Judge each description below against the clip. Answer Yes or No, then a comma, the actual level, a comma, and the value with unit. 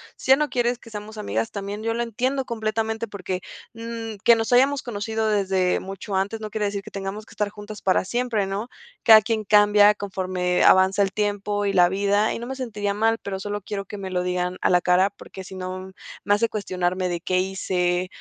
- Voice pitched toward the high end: Yes, high, 205 Hz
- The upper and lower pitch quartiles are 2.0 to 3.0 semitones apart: Yes, average, 2.7 semitones